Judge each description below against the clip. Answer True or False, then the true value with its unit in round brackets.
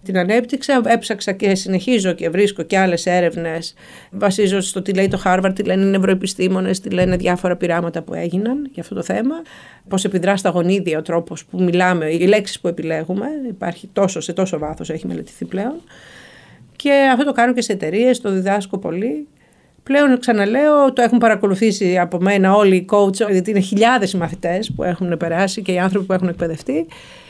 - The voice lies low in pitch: False (195 Hz)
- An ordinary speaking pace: False (185 wpm)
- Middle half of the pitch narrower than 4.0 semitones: True (3.3 semitones)